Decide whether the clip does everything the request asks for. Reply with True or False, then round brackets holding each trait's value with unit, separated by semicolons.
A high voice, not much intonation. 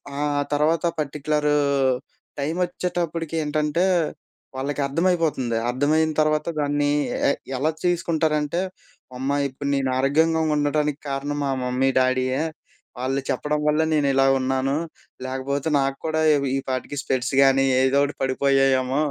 False (145 Hz; 2.3 semitones)